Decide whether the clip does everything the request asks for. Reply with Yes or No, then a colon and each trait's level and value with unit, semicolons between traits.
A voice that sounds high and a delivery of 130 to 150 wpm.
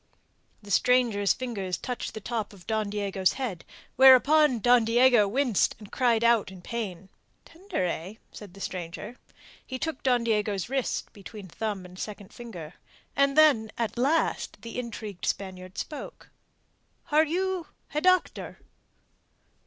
Yes: high, 225 Hz; average, 140 wpm